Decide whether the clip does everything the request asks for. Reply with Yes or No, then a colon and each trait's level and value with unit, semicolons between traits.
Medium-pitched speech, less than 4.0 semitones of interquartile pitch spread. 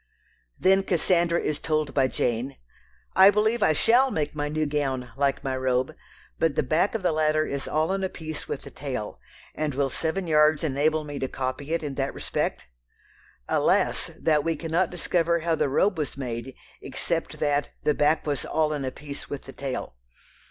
Yes: medium, 150 Hz; average, 3.0 semitones